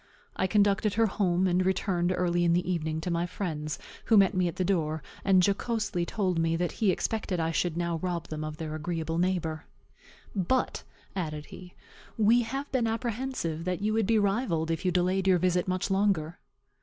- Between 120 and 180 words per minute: No, average, 195 wpm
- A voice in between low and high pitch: Yes, medium, 180 Hz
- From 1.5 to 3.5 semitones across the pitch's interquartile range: Yes, average, 3.2 semitones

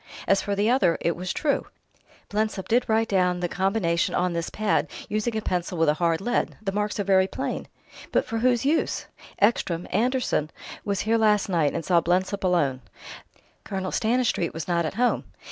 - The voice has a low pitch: No, high, 195 Hz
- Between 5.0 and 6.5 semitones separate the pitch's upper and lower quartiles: No, average, 3.9 semitones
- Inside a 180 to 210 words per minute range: Yes, average, 185 wpm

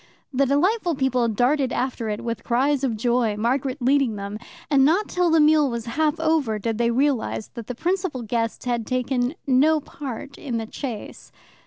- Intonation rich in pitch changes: No, average, 3.9 semitones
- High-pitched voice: Yes, very high, 255 Hz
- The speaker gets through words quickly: No, average, 180 wpm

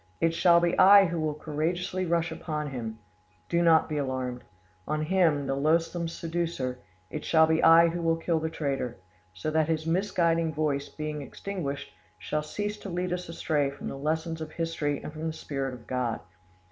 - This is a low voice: No, medium, 160 Hz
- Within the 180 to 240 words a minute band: Yes, average, 185 wpm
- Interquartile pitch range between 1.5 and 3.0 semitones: Yes, narrow, 2.6 semitones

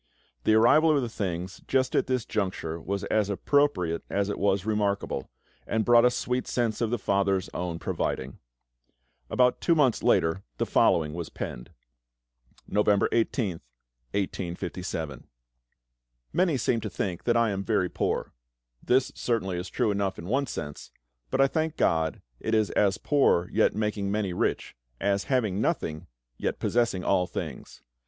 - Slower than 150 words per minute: No, average, 155 wpm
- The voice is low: Yes, low, 100 Hz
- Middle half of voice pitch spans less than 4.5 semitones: No, average, 4.8 semitones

